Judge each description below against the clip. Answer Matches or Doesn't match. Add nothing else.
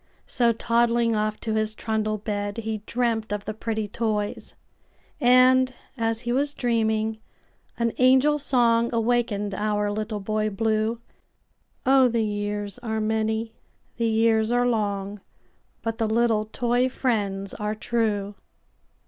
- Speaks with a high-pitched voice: Matches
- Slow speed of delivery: Matches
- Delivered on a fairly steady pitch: Matches